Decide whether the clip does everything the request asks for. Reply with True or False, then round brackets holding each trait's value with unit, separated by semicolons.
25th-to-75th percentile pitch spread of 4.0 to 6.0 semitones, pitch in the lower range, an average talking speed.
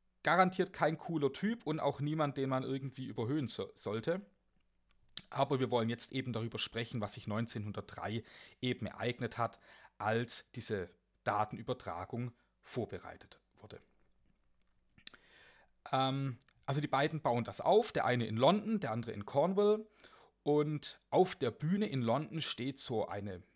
True (4.6 semitones; 130 Hz; 140 wpm)